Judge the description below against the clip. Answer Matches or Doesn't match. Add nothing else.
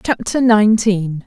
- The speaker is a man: Doesn't match